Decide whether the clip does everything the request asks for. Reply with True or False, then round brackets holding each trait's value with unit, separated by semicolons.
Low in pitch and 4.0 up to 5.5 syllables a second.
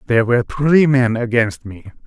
True (125 Hz; 5.1 syllables/s)